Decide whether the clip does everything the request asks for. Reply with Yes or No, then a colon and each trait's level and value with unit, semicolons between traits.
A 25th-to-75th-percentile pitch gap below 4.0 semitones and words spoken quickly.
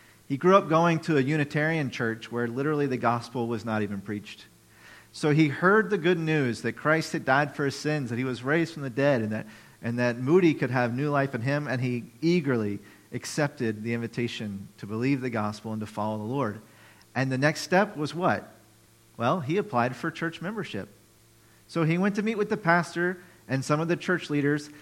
No: wide, 5.6 semitones; fast, 215 wpm